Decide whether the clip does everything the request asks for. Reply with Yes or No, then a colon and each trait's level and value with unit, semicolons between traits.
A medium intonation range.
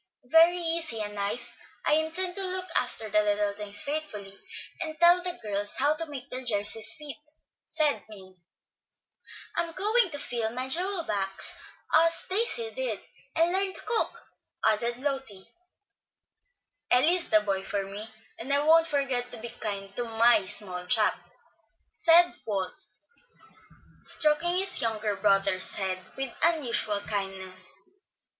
No: wide, 8.1 semitones